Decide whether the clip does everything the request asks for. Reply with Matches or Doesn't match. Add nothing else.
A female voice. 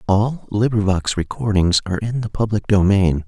Doesn't match